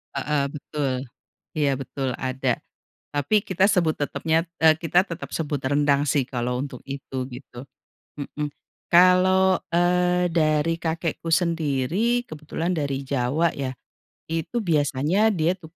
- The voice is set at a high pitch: No, medium, 150 Hz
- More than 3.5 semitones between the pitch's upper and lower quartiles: No, average, 3.2 semitones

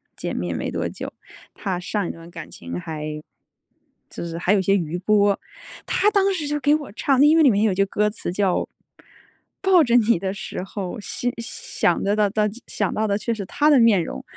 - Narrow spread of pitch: No, average, 5.3 semitones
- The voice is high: Yes, high, 205 Hz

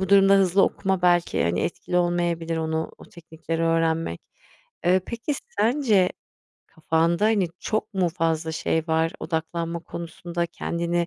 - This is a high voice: No, medium, 170 Hz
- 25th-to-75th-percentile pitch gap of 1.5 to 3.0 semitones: Yes, narrow, 2.6 semitones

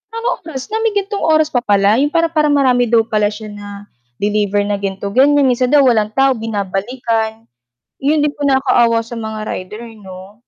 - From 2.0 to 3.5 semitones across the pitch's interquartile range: No, wide, 5.5 semitones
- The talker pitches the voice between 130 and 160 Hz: No, high, 230 Hz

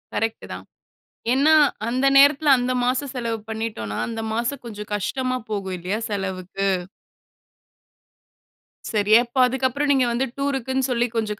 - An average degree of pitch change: Yes, average, 4.0 semitones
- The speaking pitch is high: Yes, high, 240 Hz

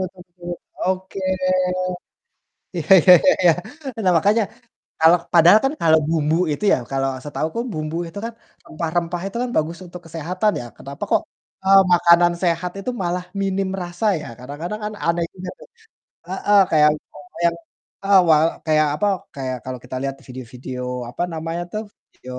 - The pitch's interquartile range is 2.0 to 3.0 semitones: No, average, 3.4 semitones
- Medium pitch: Yes, medium, 170 Hz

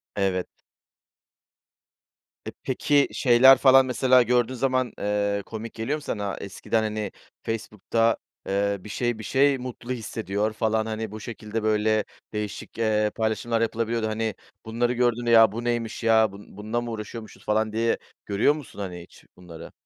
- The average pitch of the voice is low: Yes, low, 110 Hz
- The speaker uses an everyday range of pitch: No, narrow, 2.0 semitones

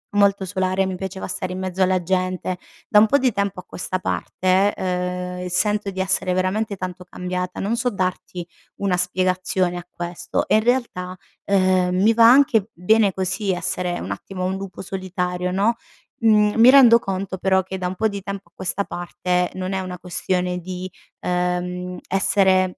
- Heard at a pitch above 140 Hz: Yes, medium, 185 Hz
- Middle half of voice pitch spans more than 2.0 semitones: No, narrow, 1.6 semitones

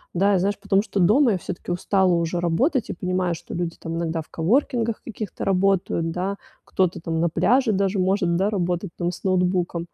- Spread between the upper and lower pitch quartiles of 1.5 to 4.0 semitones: Yes, average, 2.7 semitones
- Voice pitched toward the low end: No, medium, 185 Hz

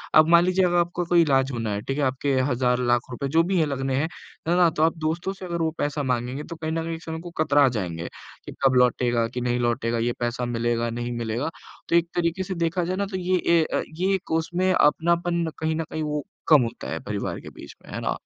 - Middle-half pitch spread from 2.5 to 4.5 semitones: No, wide, 5.5 semitones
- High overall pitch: No, medium, 155 Hz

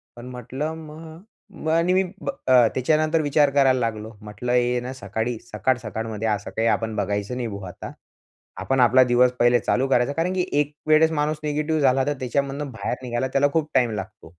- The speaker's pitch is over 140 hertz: No, low, 130 Hz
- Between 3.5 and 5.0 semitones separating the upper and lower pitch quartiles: Yes, average, 4.3 semitones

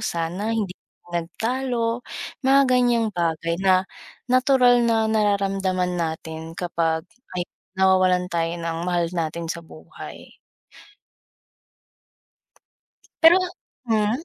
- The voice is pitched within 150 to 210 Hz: Yes, high, 190 Hz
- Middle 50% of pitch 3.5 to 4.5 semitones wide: No, average, 5.3 semitones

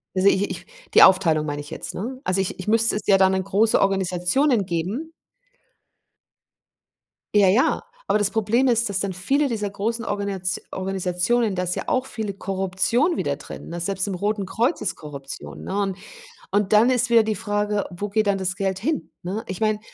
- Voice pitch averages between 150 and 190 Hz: No, high, 200 Hz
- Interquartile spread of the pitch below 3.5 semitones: Yes, average, 3.0 semitones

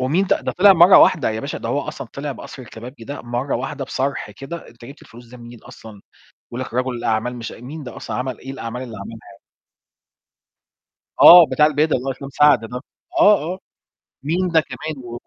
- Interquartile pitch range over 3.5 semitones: Yes, average, 4.0 semitones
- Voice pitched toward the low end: Yes, low, 130 Hz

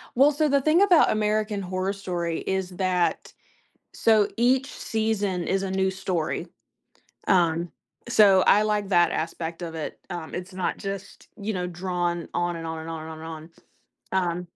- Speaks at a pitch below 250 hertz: Yes, medium, 185 Hz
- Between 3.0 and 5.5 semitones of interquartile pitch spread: Yes, average, 3.4 semitones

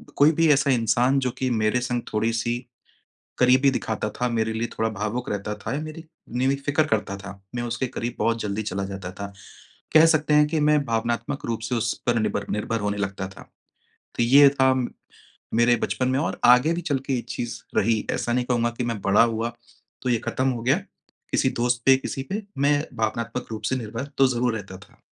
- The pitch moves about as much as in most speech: Yes, average, 3.0 semitones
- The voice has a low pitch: Yes, low, 120 Hz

